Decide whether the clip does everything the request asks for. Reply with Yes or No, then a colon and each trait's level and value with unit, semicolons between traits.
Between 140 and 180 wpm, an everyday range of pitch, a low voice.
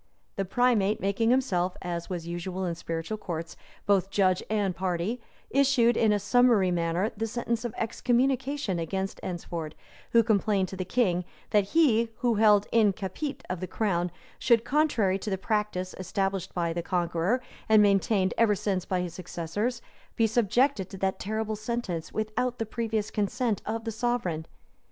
No: average, 165 wpm; average, 4.0 semitones; high, 205 Hz